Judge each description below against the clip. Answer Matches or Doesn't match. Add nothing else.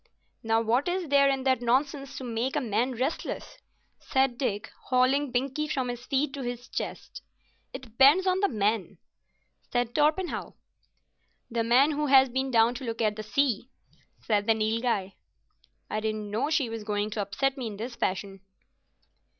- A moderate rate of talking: Matches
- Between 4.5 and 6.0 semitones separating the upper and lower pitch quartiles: Doesn't match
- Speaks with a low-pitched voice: Doesn't match